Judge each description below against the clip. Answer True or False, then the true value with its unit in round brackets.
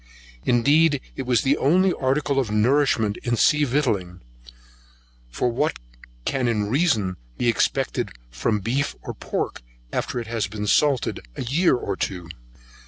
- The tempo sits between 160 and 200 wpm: False (145 wpm)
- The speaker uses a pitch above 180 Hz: False (125 Hz)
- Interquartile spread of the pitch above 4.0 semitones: True (5.1 semitones)